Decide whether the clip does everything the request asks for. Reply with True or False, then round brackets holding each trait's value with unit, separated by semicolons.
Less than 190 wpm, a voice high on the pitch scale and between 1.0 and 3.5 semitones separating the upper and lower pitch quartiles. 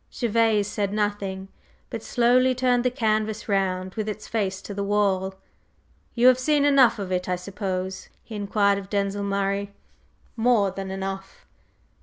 True (155 wpm; 205 Hz; 2.9 semitones)